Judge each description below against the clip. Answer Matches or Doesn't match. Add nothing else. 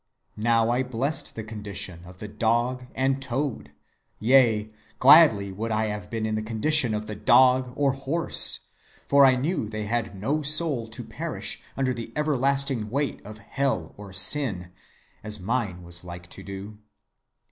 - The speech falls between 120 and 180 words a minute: Matches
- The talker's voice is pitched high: Doesn't match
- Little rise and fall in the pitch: Doesn't match